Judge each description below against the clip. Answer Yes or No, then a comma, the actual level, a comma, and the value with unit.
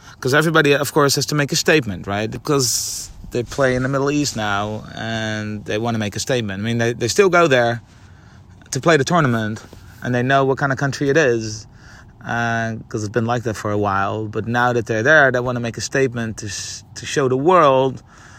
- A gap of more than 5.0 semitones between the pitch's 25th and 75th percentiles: No, average, 3.9 semitones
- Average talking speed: No, fast, 230 wpm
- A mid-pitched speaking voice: No, low, 115 Hz